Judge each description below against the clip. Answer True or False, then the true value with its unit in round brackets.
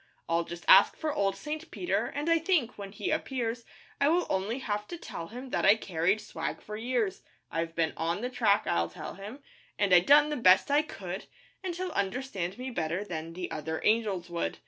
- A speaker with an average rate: False (210 wpm)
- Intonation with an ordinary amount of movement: False (6.9 semitones)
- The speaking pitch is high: True (210 Hz)